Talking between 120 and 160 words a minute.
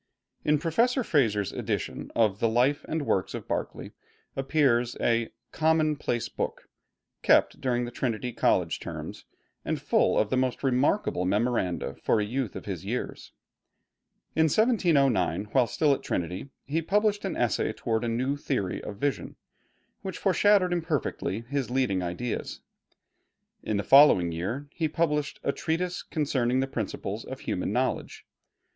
Yes: average, 145 wpm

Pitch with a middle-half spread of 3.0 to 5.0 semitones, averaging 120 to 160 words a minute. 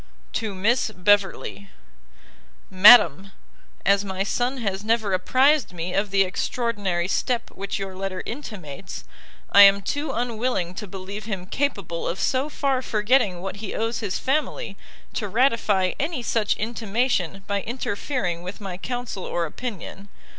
Yes: average, 4.0 semitones; average, 140 wpm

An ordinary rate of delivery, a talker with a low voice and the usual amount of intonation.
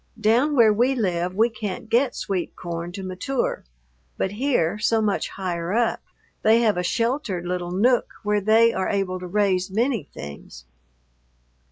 No: average, 160 wpm; high, 205 Hz; average, 4.1 semitones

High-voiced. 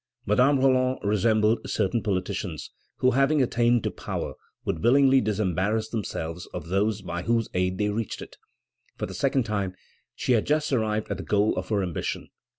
No: low, 110 Hz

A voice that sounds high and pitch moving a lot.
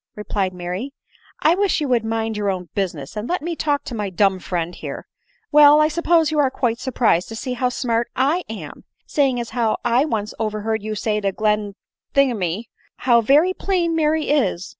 Yes: high, 230 Hz; wide, 5.8 semitones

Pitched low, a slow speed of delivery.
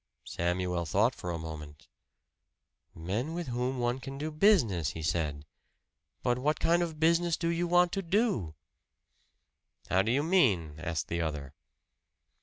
No: low, 120 Hz; average, 150 wpm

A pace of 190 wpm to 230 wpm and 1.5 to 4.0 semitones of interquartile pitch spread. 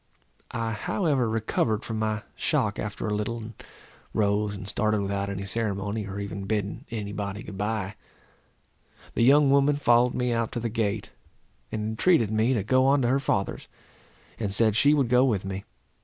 No: average, 180 wpm; average, 2.9 semitones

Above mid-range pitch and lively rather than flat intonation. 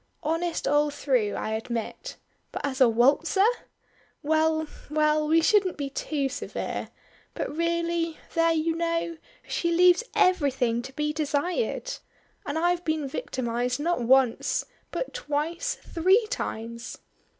No: very high, 310 Hz; average, 4.0 semitones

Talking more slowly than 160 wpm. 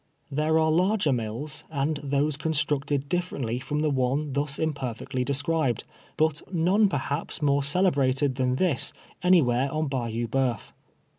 Yes: average, 140 wpm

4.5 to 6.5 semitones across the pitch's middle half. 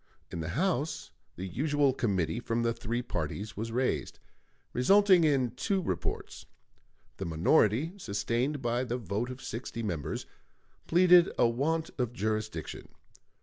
Yes: wide, 5.5 semitones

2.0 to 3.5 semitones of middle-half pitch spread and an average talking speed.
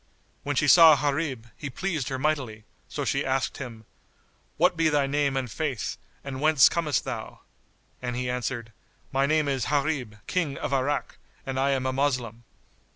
Yes: average, 2.8 semitones; average, 170 wpm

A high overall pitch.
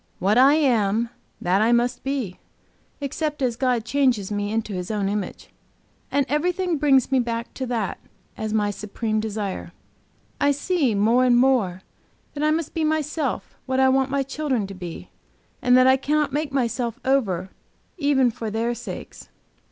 Yes: very high, 250 Hz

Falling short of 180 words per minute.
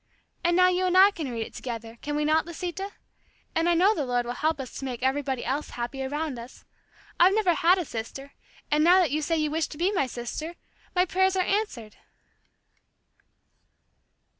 No: average, 200 wpm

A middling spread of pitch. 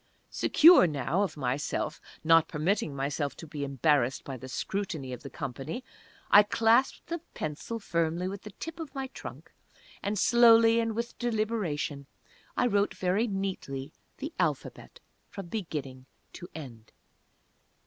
No: wide, 7.9 semitones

